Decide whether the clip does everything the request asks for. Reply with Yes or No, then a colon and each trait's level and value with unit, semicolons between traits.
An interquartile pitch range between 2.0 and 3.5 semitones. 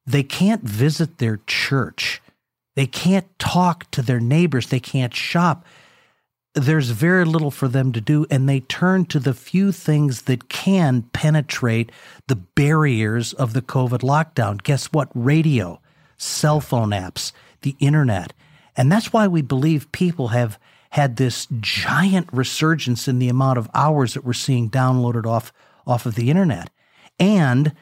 No: average, 3.9 semitones